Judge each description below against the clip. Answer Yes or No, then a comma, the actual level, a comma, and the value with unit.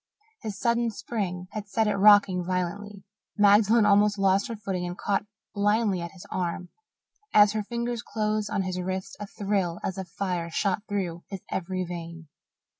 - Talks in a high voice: Yes, high, 200 Hz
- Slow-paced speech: No, average, 170 wpm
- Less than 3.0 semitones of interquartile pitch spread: Yes, narrow, 2.4 semitones